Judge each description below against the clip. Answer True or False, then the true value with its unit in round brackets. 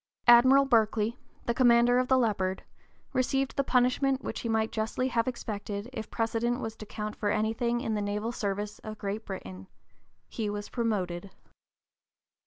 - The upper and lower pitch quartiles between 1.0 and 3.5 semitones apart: True (2.8 semitones)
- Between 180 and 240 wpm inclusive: False (160 wpm)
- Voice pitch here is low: False (225 Hz)